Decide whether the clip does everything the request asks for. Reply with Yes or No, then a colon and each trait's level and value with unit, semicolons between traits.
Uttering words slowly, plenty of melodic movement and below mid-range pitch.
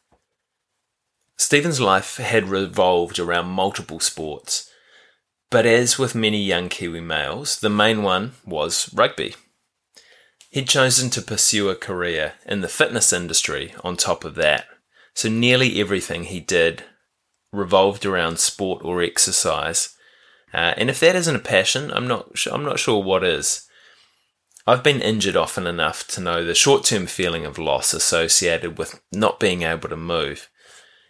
No: average, 150 wpm; wide, 5.9 semitones; low, 105 Hz